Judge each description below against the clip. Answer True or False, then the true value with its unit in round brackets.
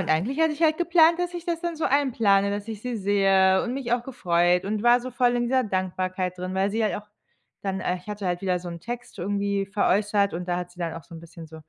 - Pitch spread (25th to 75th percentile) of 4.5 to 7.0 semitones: True (5.1 semitones)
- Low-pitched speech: False (200 Hz)